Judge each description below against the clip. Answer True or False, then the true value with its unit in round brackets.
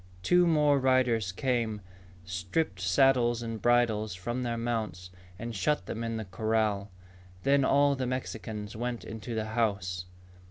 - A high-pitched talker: False (115 Hz)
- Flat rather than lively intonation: False (3.4 semitones)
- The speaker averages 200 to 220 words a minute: False (145 wpm)